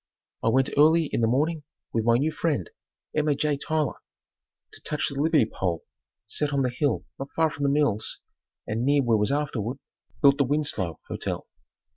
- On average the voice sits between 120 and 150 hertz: Yes, medium, 140 Hz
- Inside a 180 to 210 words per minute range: Yes, average, 185 wpm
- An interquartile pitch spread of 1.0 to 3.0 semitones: No, average, 4.3 semitones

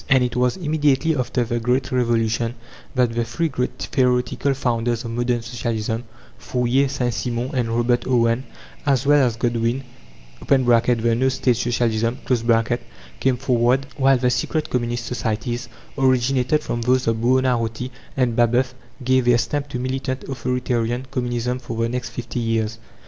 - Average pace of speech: Yes, average, 150 wpm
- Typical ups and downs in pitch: No, narrow, 1.8 semitones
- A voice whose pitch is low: Yes, low, 125 Hz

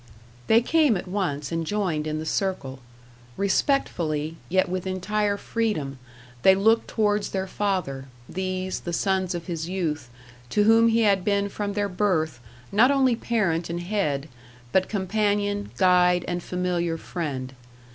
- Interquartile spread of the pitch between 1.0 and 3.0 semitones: No, average, 3.8 semitones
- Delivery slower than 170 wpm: Yes, average, 145 wpm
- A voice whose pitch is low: No, medium, 185 Hz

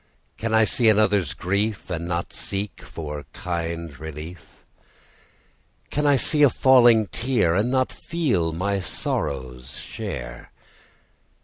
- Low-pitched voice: Yes, very low, 95 Hz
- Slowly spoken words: Yes, slow, 120 wpm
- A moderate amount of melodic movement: No, wide, 5.7 semitones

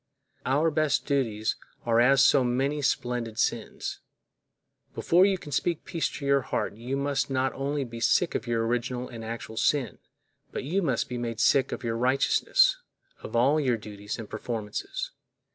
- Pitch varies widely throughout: No, average, 3.4 semitones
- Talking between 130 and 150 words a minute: No, average, 170 wpm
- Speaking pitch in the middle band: No, low, 130 Hz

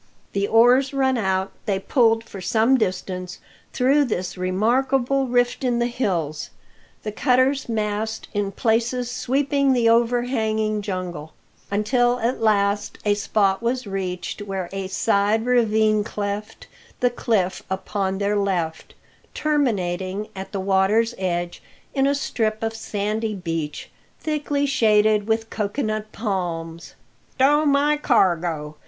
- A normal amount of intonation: Yes, average, 4.2 semitones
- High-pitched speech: Yes, high, 215 Hz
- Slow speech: Yes, slow, 130 wpm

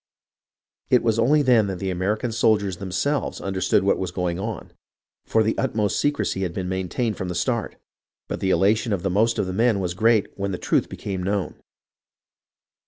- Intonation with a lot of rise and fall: No, average, 3.3 semitones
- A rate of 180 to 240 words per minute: Yes, average, 190 wpm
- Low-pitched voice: Yes, low, 100 Hz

